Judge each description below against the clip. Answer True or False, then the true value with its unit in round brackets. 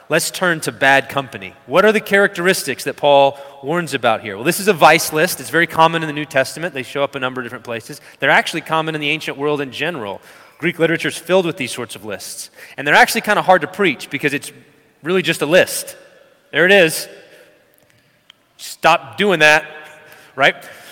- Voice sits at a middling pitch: True (155 Hz)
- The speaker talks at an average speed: False (210 wpm)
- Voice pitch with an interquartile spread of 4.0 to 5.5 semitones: False (3.5 semitones)